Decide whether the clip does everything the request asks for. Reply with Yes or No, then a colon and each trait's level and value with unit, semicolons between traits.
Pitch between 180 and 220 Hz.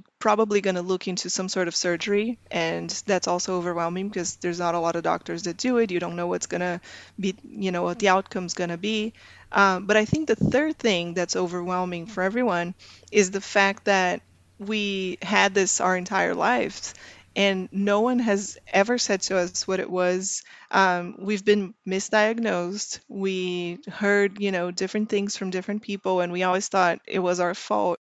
Yes: high, 190 Hz